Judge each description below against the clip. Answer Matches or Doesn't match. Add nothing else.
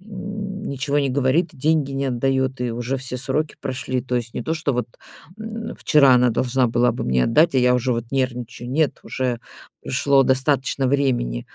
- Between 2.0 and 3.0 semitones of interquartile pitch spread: Matches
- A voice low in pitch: Matches